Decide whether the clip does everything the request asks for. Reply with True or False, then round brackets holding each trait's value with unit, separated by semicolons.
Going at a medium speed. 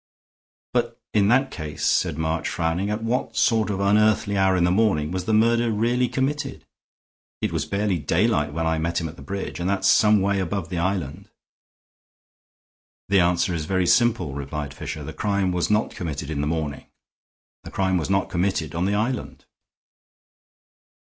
True (175 wpm)